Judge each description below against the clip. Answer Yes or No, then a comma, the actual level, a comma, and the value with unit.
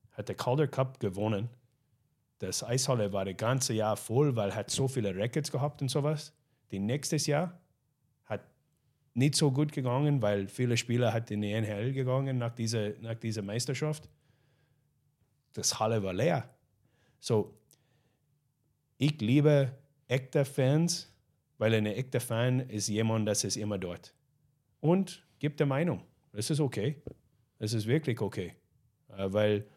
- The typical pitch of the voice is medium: No, low, 125 Hz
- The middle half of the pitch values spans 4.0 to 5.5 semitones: Yes, average, 4.8 semitones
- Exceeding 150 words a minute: No, average, 145 wpm